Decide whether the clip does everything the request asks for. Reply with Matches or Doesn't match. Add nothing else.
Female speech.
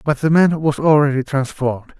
Doesn't match